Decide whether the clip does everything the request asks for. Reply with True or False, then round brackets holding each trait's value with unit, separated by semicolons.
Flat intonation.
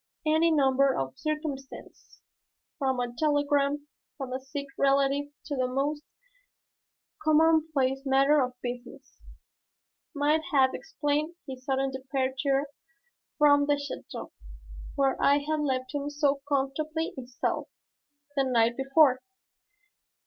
True (1.9 semitones)